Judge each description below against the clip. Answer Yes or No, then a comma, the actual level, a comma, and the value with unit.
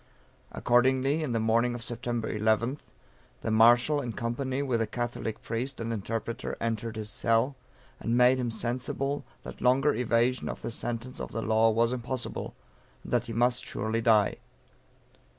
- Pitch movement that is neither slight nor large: No, narrow, 1.9 semitones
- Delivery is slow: No, average, 160 wpm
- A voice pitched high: No, low, 120 Hz